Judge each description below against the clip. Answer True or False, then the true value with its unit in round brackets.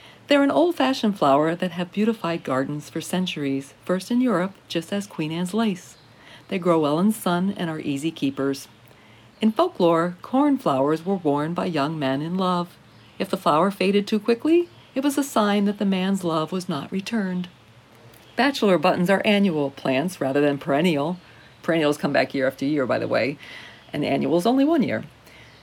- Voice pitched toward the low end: False (175 Hz)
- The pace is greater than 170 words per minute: True (185 wpm)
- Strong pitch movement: True (5.9 semitones)